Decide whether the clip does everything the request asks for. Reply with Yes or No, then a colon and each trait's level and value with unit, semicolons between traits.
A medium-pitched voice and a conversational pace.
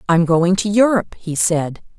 Yes: medium, 180 Hz; average, 180 wpm